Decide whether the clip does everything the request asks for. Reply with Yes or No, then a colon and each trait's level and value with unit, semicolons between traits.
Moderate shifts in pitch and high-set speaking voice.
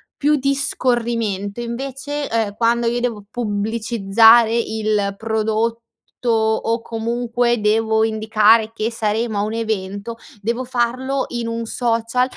No: narrow, 1.6 semitones; high, 230 Hz